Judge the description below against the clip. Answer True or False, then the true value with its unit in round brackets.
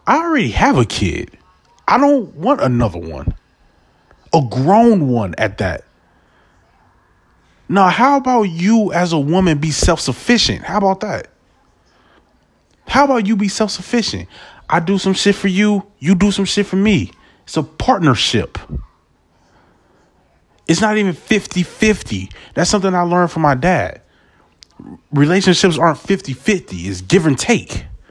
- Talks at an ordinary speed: True (145 wpm)